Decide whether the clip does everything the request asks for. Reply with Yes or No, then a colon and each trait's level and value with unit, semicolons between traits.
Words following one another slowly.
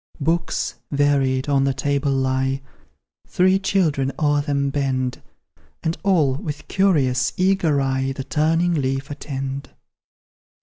Yes: slow, 120 wpm